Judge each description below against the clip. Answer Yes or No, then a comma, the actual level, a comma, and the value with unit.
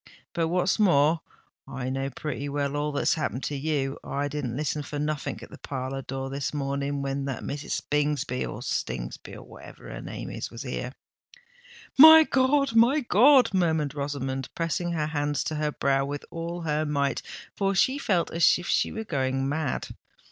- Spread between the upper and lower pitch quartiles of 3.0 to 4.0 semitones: Yes, average, 3.5 semitones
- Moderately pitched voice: Yes, medium, 145 Hz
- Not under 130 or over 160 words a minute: No, average, 175 wpm